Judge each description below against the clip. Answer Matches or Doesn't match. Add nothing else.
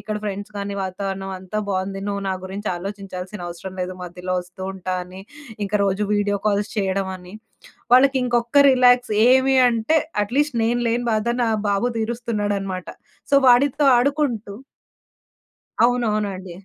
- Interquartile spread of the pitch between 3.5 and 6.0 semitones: Matches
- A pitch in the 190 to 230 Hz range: Matches